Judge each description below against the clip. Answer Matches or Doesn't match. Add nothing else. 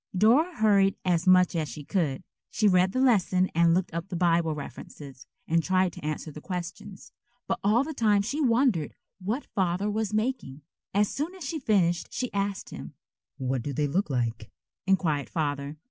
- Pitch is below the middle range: Doesn't match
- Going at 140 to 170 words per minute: Doesn't match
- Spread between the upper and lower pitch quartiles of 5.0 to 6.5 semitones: Matches